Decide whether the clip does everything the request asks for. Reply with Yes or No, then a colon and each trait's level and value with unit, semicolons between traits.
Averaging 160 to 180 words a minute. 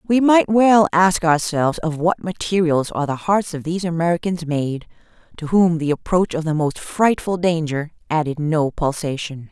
Yes: average, 170 wpm